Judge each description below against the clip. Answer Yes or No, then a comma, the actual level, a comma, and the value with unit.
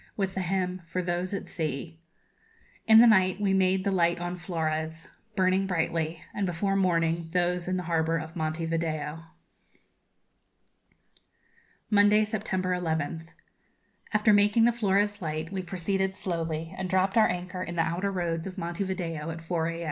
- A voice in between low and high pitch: Yes, medium, 180 Hz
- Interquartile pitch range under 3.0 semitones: Yes, narrow, 2.6 semitones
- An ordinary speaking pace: Yes, average, 160 wpm